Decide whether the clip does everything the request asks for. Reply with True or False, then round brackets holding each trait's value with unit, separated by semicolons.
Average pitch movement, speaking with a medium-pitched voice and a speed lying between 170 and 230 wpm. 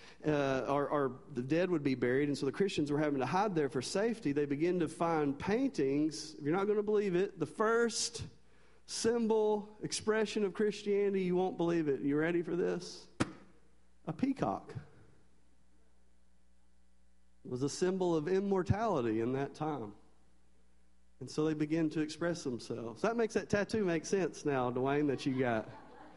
False (7.2 semitones; 150 Hz; 175 wpm)